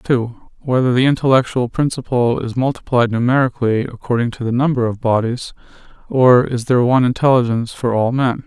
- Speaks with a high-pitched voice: No, low, 125 Hz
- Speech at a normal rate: Yes, average, 155 wpm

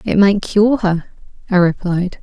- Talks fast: No, average, 160 wpm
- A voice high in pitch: Yes, high, 195 Hz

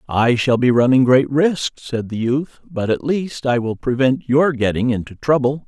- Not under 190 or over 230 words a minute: Yes, average, 200 wpm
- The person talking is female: No, male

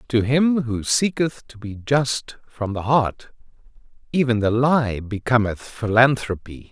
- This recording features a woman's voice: No, male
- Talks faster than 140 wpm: No, slow, 135 wpm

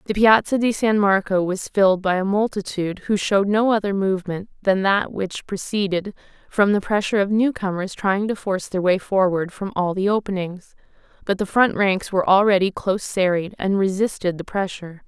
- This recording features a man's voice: No, female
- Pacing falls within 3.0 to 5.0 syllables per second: No, 5.4 syllables/s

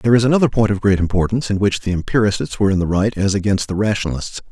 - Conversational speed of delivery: No, fast, 255 wpm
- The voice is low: Yes, low, 105 Hz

